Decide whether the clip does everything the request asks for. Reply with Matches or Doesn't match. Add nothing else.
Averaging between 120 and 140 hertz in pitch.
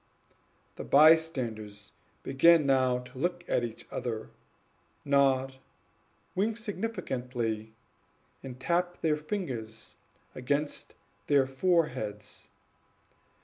Matches